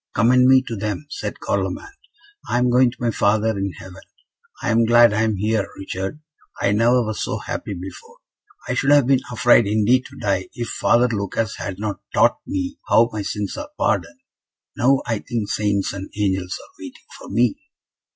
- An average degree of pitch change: Yes, average, 3.4 semitones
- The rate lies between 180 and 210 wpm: Yes, average, 190 wpm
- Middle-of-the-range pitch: No, low, 110 Hz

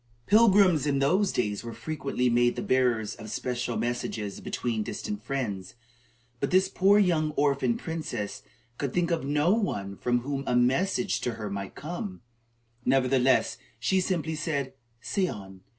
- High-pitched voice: No, low, 135 Hz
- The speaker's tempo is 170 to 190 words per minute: No, average, 150 wpm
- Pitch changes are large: Yes, wide, 6.5 semitones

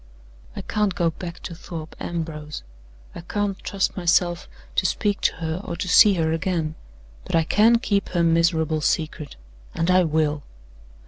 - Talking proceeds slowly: No, average, 165 wpm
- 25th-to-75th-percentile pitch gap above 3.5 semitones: No, narrow, 2.6 semitones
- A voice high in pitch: No, medium, 170 Hz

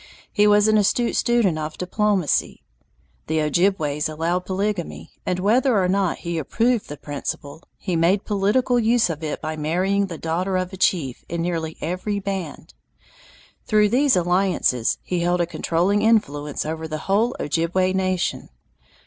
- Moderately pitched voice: Yes, medium, 180 Hz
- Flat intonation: No, average, 4.2 semitones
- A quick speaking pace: No, average, 155 wpm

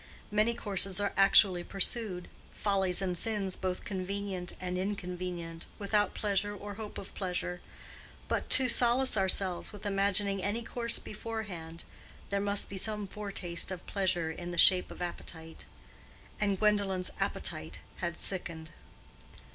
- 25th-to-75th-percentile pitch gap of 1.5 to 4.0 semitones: Yes, narrow, 2.5 semitones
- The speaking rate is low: Yes, slow, 130 wpm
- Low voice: No, high, 195 Hz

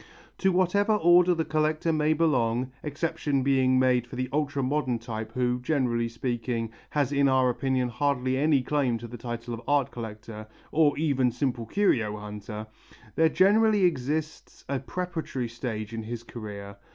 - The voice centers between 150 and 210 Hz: No, low, 130 Hz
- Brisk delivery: No, average, 160 wpm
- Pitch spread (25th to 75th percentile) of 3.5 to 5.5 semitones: Yes, average, 4.6 semitones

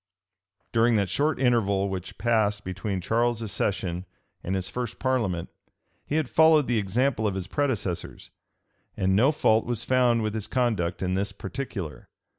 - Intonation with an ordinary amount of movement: Yes, average, 4.3 semitones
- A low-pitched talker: Yes, low, 110 Hz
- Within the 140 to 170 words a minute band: Yes, average, 155 wpm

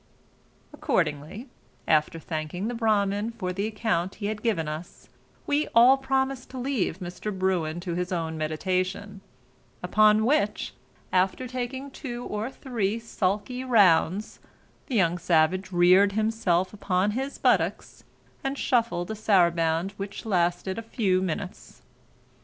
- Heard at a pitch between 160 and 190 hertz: No, high, 200 Hz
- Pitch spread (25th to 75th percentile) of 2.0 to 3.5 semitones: No, average, 4.5 semitones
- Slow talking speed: Yes, slow, 130 wpm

